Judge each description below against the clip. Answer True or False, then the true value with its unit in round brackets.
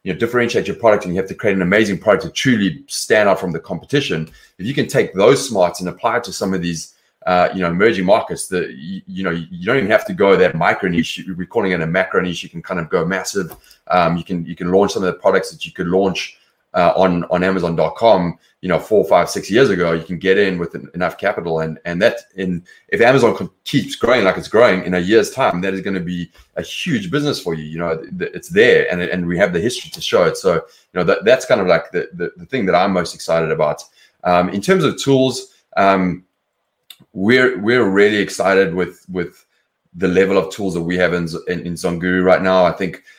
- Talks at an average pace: False (250 wpm)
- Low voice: True (95 Hz)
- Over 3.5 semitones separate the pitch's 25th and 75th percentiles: False (2.5 semitones)